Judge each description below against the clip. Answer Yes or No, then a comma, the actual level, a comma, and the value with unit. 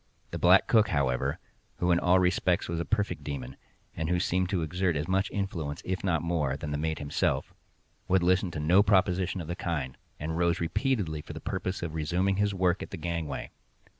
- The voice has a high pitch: No, very low, 85 Hz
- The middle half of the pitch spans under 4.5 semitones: Yes, average, 3.1 semitones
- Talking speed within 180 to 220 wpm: Yes, fast, 205 wpm